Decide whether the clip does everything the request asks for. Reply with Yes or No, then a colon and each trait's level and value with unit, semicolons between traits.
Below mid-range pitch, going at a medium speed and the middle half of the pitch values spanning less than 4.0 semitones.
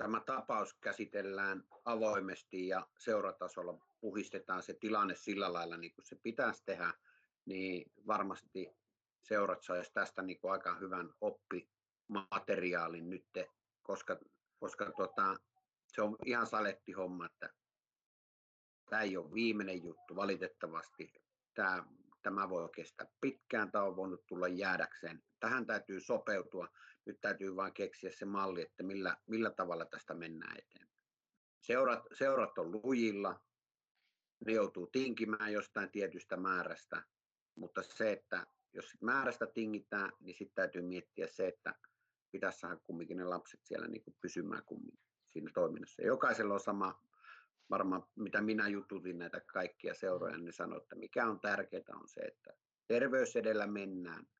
No: low, 100 Hz; average, 135 wpm; average, 4.3 semitones